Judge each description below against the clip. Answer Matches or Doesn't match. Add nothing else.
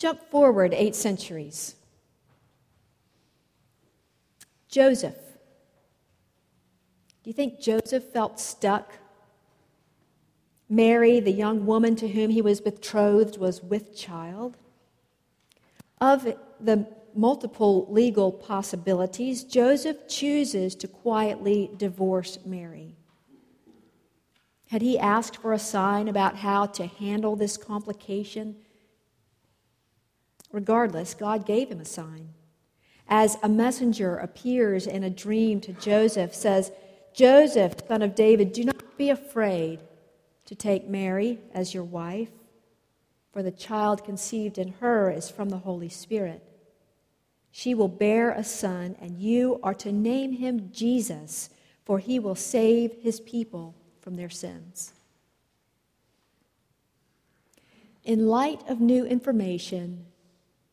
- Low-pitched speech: Doesn't match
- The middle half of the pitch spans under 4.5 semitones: Matches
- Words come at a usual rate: Doesn't match